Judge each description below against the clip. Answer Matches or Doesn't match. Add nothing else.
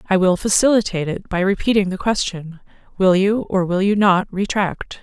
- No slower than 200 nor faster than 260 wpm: Doesn't match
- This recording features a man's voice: Doesn't match